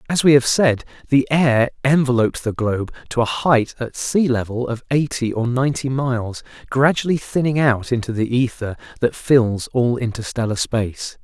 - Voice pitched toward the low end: Yes, low, 125 Hz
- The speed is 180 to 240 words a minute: No, average, 160 wpm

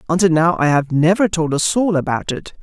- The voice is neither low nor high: Yes, medium, 165 Hz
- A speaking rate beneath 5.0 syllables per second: No, 5.6 syllables/s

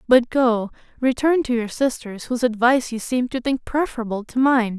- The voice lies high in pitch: Yes, high, 245 Hz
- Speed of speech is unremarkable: Yes, average, 190 wpm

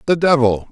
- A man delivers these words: Yes, male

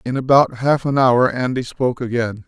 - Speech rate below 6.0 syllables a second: Yes, 5.1 syllables/s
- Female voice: No, male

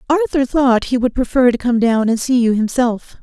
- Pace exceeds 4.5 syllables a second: Yes, 5.0 syllables/s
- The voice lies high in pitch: Yes, high, 245 Hz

